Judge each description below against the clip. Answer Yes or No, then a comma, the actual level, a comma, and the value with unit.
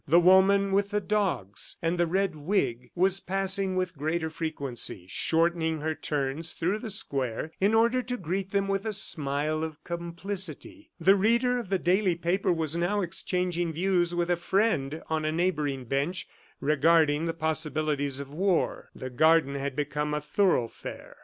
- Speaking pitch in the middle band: Yes, medium, 170 Hz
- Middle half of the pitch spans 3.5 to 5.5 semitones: Yes, average, 4.3 semitones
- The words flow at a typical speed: Yes, average, 165 wpm